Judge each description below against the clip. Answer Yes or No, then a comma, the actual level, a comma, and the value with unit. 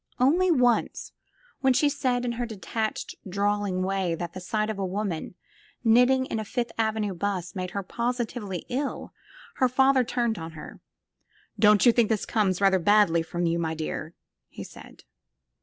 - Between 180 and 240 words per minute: No, average, 170 wpm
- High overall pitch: Yes, high, 210 Hz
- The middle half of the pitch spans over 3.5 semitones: Yes, average, 4.7 semitones